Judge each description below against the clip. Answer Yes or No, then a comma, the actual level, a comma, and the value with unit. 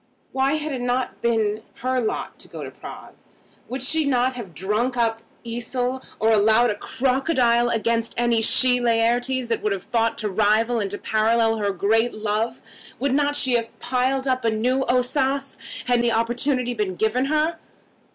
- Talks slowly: No, average, 170 wpm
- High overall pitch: Yes, high, 240 Hz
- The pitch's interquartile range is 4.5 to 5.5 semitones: No, narrow, 2.5 semitones